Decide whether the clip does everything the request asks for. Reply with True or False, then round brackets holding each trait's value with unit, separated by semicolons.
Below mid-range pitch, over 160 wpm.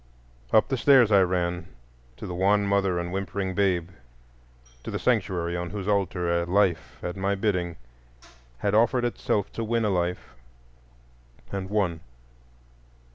False (95 Hz; 145 wpm)